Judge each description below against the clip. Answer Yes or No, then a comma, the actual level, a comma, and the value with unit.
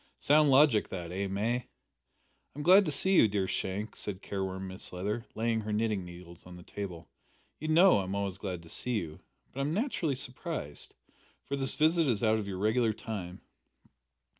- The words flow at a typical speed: Yes, average, 185 wpm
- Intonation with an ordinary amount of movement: No, wide, 6.5 semitones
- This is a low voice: Yes, low, 105 Hz